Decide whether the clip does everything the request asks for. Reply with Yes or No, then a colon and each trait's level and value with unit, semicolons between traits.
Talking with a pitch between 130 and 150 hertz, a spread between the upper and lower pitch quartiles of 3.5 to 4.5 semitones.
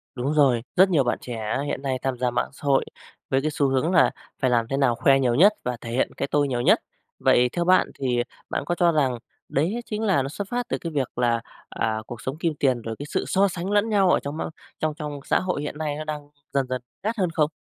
No: medium, 140 Hz; average, 5.1 semitones